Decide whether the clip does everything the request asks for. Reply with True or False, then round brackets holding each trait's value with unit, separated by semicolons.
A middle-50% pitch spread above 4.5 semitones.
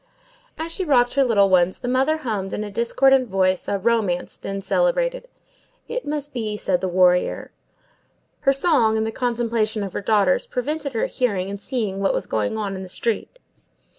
True (5.6 semitones)